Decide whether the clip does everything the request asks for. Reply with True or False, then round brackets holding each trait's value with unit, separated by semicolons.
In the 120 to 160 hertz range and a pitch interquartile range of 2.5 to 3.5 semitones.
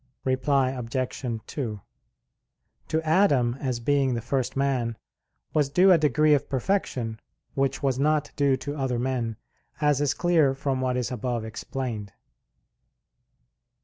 True (135 Hz; 2.9 semitones)